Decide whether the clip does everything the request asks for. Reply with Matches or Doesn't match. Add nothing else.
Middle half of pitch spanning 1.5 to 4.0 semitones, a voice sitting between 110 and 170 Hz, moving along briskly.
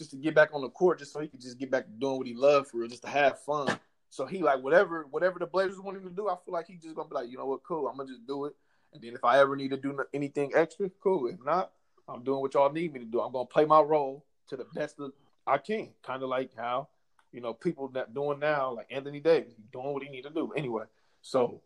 Matches